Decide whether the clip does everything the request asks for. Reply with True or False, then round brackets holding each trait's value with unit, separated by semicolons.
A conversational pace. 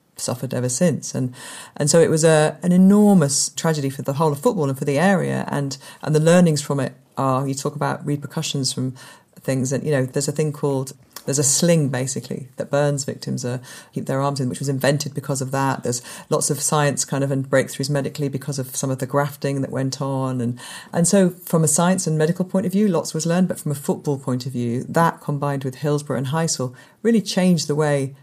False (230 wpm)